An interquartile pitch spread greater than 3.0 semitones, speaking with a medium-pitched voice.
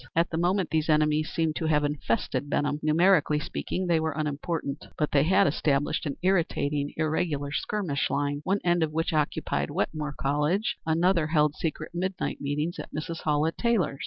No: average, 2.7 semitones; medium, 155 Hz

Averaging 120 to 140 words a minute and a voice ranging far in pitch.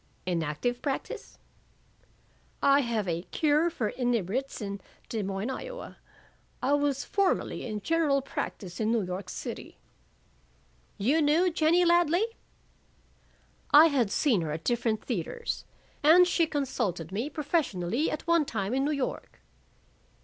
Yes: slow, 135 wpm; wide, 7.1 semitones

